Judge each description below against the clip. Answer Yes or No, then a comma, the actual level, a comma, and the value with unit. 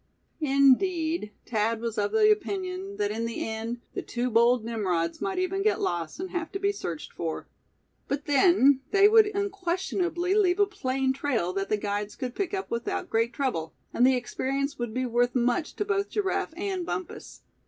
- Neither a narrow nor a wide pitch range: No, wide, 8.7 semitones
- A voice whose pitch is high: Yes, very high, 275 Hz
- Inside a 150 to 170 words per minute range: No, average, 185 wpm